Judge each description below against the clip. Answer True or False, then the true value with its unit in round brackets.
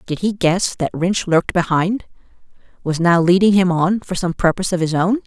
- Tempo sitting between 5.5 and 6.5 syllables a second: False (5.3 syllables/s)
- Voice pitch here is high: False (180 Hz)